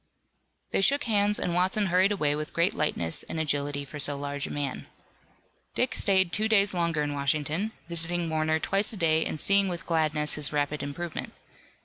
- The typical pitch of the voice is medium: Yes, medium, 165 Hz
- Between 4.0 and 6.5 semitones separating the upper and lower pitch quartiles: Yes, average, 4.5 semitones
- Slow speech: No, average, 180 wpm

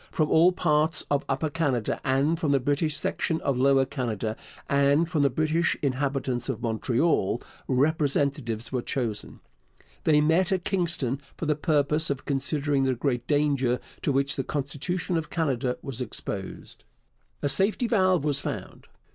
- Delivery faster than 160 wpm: No, average, 155 wpm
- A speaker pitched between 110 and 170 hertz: Yes, medium, 140 Hz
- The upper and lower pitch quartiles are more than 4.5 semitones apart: No, average, 3.2 semitones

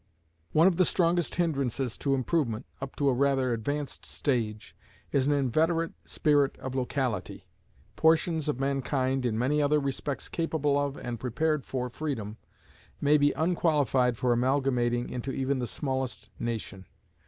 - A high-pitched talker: No, low, 135 Hz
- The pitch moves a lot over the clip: No, average, 3.2 semitones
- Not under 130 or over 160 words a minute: Yes, average, 145 wpm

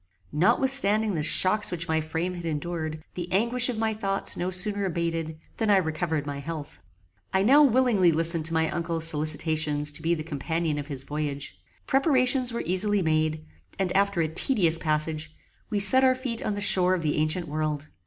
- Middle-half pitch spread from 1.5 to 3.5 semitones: No, average, 4.8 semitones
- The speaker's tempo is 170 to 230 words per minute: Yes, average, 185 wpm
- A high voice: No, medium, 170 Hz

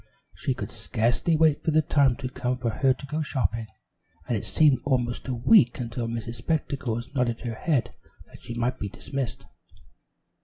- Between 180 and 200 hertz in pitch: No, low, 125 Hz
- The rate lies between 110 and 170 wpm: No, average, 180 wpm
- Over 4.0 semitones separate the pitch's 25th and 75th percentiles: No, average, 3.2 semitones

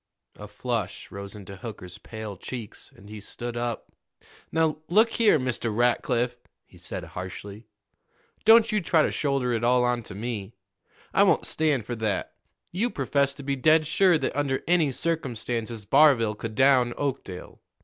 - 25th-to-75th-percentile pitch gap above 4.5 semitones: Yes, average, 5.3 semitones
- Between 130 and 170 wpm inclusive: Yes, average, 160 wpm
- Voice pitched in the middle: No, low, 125 Hz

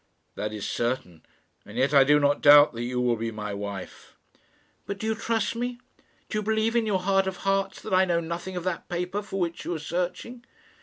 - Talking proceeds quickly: Yes, fast, 220 wpm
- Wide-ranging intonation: Yes, wide, 7.7 semitones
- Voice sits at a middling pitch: Yes, medium, 175 Hz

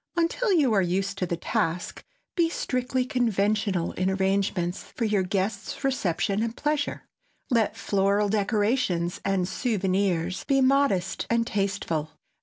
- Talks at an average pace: No, slow, 130 wpm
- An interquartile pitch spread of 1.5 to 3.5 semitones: No, average, 4.8 semitones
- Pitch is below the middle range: No, high, 200 Hz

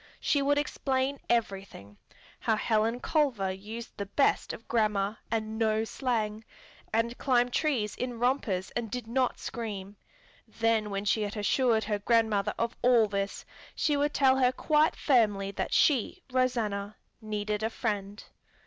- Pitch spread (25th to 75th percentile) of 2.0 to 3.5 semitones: Yes, average, 3.2 semitones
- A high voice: Yes, high, 225 Hz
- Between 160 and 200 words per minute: No, average, 150 wpm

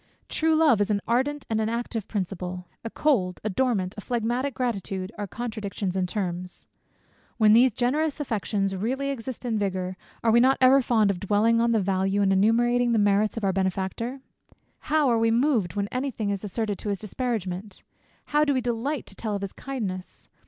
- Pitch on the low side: No, high, 220 Hz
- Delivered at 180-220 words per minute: Yes, average, 195 wpm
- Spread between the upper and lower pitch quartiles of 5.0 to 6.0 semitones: No, average, 3.9 semitones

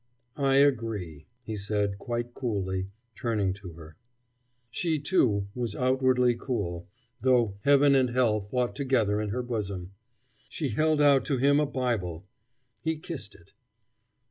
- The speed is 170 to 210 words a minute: No, average, 140 wpm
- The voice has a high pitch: No, low, 120 Hz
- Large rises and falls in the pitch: No, average, 4.9 semitones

